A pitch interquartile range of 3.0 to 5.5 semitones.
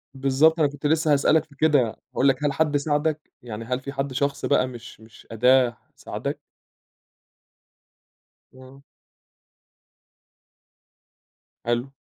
No: narrow, 2.5 semitones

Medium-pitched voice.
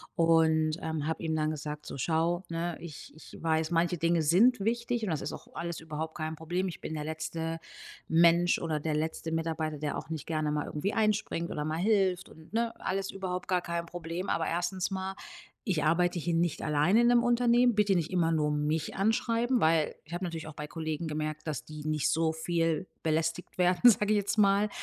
Yes: medium, 165 Hz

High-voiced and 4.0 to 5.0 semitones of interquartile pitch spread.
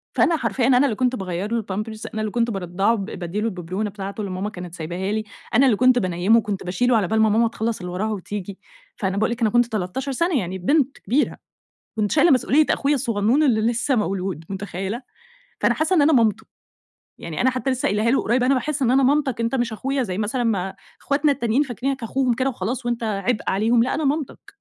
Yes: high, 225 Hz; average, 4.6 semitones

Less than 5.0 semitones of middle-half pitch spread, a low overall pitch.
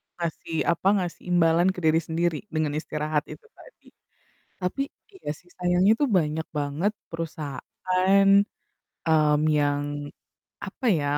No: average, 3.0 semitones; medium, 165 Hz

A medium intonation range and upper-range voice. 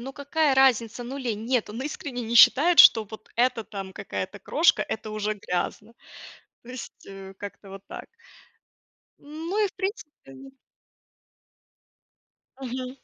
Yes: average, 4.6 semitones; high, 245 Hz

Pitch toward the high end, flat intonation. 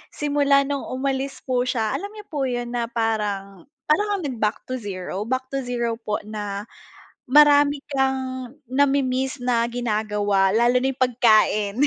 No: very high, 250 Hz; average, 3.8 semitones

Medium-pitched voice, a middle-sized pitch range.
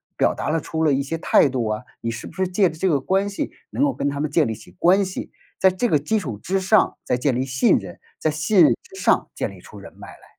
No: medium, 160 Hz; wide, 5.9 semitones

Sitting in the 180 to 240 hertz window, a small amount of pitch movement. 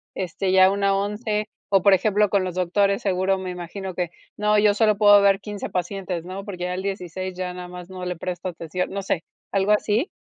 Yes: high, 190 Hz; narrow, 2.0 semitones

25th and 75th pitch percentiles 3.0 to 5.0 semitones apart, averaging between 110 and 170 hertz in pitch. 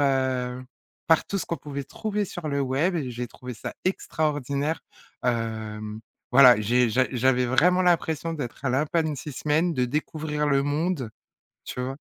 Yes: average, 4.0 semitones; medium, 140 Hz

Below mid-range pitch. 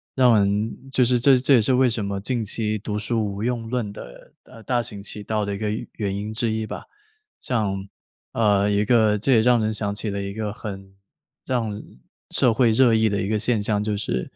Yes: low, 110 Hz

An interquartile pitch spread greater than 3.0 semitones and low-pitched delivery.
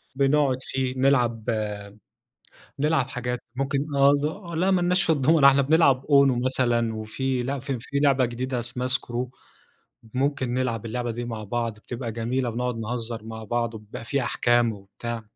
No: average, 2.7 semitones; low, 125 Hz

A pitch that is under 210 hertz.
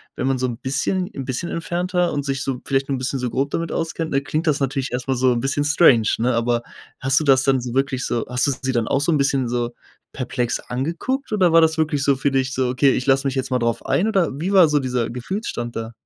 Yes: low, 135 Hz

